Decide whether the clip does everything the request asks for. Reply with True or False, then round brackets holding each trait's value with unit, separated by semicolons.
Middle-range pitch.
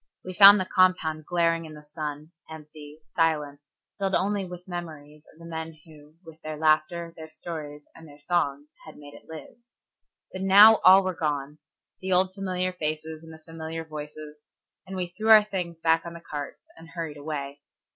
True (160 Hz)